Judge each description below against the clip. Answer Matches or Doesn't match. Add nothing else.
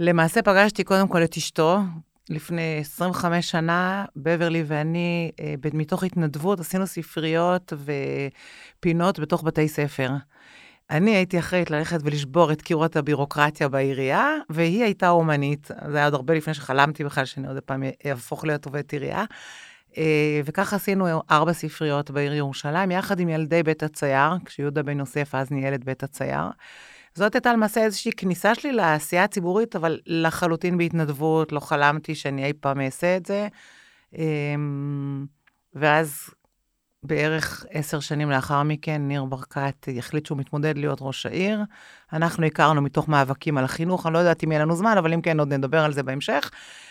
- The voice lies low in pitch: Doesn't match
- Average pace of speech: Doesn't match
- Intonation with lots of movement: Doesn't match